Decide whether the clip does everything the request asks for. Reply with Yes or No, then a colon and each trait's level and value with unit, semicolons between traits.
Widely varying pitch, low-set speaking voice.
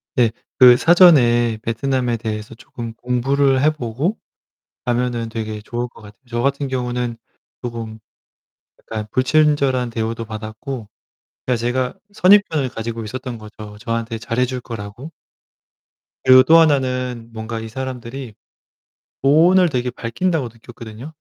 No: average, 2.7 semitones; low, 120 Hz